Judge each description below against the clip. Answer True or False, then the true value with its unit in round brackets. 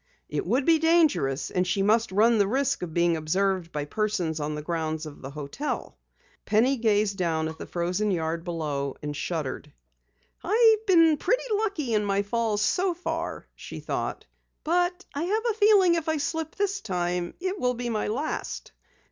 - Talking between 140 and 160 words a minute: False (180 wpm)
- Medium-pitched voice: False (215 Hz)